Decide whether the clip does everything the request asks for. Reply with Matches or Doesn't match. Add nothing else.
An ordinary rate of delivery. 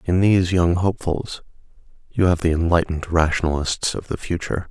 Matches